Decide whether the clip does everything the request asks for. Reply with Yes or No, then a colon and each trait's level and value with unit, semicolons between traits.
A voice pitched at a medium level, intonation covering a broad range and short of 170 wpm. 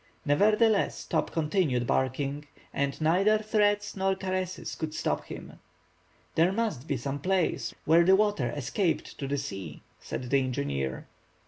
Yes: medium, 155 Hz; wide, 6.4 semitones; average, 140 wpm